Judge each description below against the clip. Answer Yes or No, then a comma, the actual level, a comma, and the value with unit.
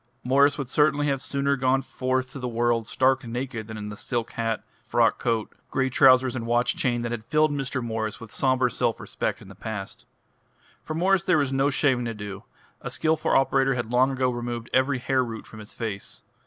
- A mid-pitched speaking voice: No, low, 125 Hz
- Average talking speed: No, fast, 210 wpm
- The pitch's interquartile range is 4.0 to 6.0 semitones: No, average, 2.7 semitones